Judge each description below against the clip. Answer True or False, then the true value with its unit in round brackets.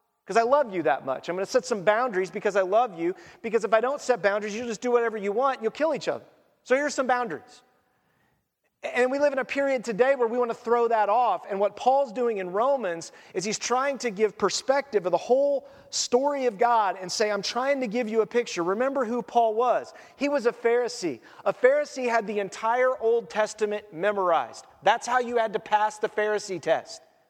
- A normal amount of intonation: True (3.4 semitones)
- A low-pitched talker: False (235 Hz)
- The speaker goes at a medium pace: False (220 wpm)